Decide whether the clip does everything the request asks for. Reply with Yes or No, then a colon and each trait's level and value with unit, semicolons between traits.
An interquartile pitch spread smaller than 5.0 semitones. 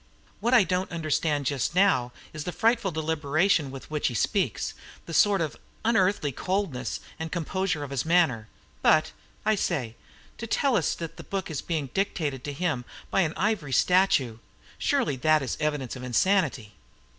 No: average, 5.3 semitones